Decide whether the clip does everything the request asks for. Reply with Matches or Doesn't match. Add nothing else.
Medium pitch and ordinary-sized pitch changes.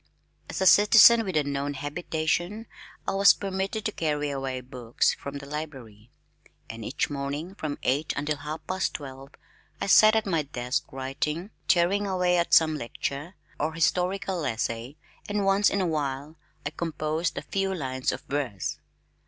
Matches